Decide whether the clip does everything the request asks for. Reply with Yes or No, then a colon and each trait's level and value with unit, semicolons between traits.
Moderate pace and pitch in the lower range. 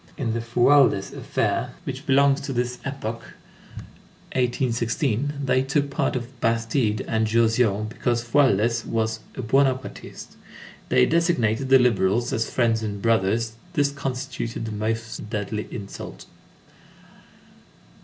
No: slow, 120 wpm; low, 115 Hz